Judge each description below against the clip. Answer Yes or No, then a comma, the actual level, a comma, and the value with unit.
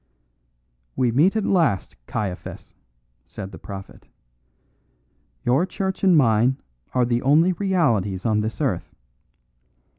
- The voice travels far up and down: Yes, wide, 8.5 semitones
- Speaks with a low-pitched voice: Yes, low, 125 Hz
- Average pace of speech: No, slow, 115 wpm